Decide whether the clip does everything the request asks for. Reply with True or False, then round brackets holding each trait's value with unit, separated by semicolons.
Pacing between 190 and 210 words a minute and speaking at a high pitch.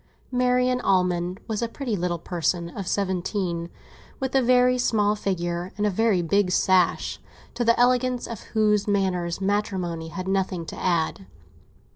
False (150 wpm; 195 Hz)